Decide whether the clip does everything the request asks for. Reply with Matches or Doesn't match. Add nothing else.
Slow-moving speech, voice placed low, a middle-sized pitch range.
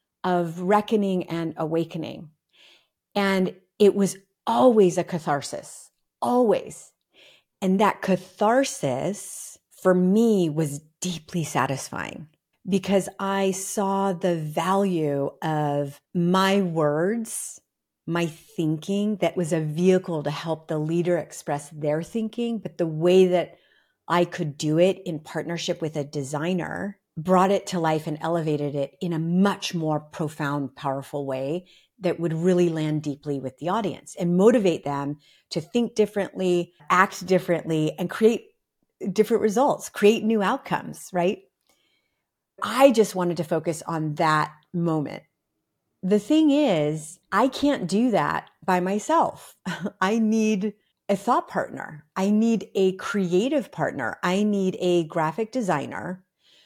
Doesn't match